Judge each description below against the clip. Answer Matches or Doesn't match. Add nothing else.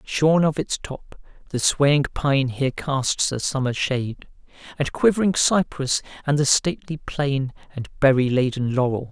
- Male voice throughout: Matches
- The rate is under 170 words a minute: Matches